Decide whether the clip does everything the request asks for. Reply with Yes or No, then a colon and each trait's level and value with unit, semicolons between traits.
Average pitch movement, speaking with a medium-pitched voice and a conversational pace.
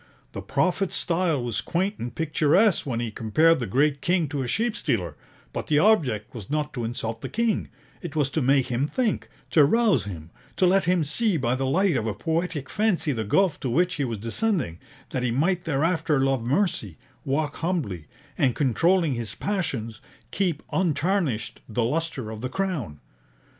No: wide, 7.0 semitones; medium, 145 Hz; average, 185 wpm